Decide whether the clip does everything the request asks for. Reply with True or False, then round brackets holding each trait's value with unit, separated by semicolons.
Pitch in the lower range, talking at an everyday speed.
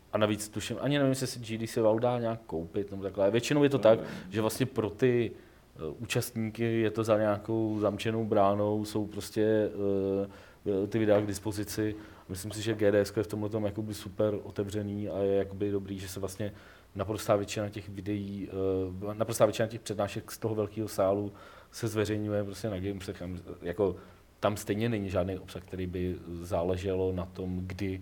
False (105 Hz; 180 wpm)